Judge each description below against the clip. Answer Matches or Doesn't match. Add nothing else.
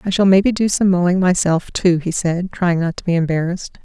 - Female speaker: Matches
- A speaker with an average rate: Doesn't match